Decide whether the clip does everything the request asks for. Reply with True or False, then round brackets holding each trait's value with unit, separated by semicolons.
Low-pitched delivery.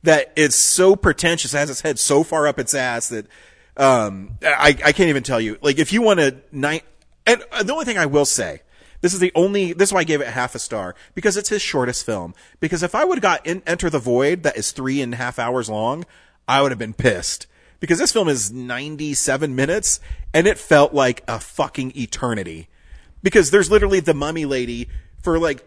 False (145 Hz)